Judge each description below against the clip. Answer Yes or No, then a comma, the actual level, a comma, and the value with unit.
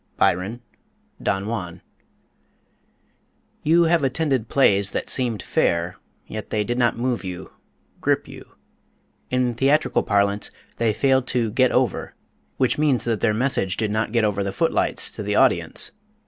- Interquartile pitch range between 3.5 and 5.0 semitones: Yes, average, 4.3 semitones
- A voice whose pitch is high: No, low, 115 Hz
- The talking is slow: No, average, 150 wpm